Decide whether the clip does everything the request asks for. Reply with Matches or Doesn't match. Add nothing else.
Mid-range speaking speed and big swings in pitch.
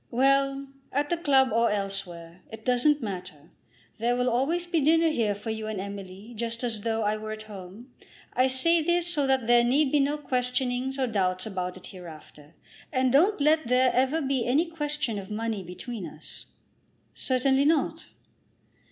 Doesn't match